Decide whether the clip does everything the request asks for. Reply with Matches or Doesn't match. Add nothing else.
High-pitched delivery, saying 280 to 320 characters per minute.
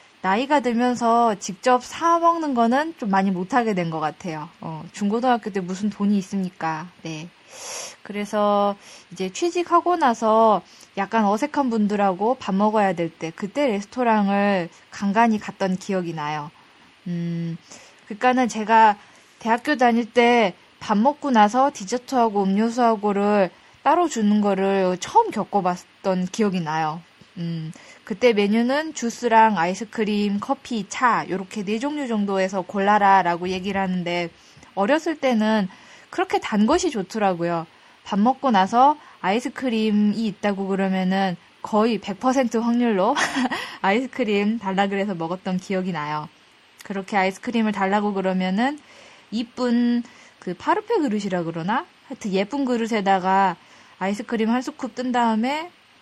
Matches